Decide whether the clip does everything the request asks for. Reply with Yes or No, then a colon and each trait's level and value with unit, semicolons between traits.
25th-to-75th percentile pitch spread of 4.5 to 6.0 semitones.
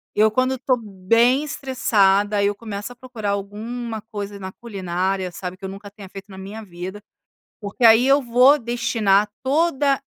No: average, 3.8 semitones